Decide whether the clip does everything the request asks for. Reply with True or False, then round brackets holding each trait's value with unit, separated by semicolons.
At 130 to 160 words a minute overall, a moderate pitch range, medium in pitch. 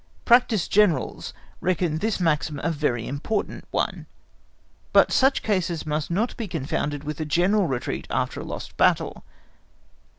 False (140 wpm; 5.7 semitones; 170 Hz)